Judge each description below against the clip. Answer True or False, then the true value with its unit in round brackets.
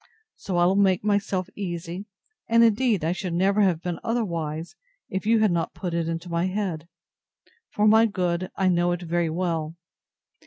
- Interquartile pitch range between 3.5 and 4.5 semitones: False (3.0 semitones)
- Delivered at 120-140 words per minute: False (170 wpm)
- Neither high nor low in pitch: True (180 Hz)